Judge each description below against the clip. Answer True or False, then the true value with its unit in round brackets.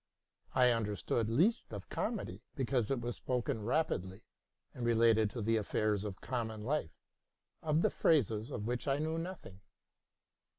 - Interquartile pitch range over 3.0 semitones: True (4.1 semitones)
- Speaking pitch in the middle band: False (115 Hz)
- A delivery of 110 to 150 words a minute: True (145 wpm)